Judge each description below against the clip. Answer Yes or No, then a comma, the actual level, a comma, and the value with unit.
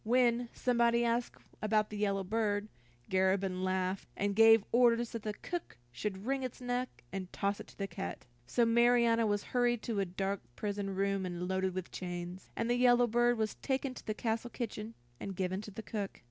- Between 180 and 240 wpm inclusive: Yes, average, 195 wpm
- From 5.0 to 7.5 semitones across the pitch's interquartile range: No, average, 3.6 semitones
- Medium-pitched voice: No, high, 215 Hz